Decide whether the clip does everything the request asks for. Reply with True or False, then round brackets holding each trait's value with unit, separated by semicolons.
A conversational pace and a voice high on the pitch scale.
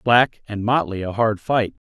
False (190 wpm; 110 Hz)